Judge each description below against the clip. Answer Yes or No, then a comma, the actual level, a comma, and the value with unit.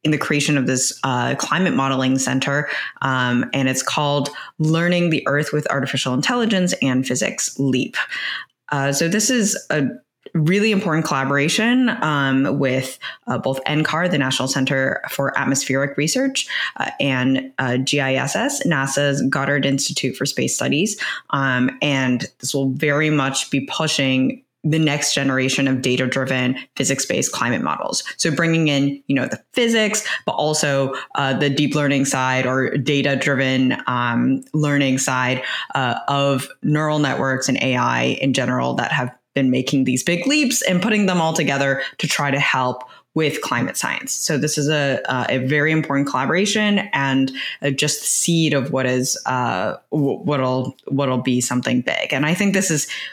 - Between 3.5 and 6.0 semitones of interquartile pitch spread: No, narrow, 2.6 semitones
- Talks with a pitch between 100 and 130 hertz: No, medium, 140 Hz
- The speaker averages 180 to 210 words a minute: No, average, 160 wpm